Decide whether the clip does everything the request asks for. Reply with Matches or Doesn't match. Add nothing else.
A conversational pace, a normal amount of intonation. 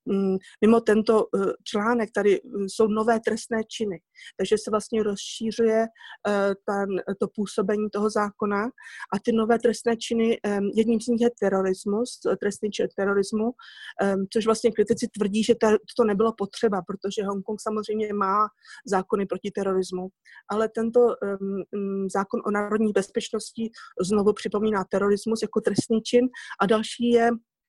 Doesn't match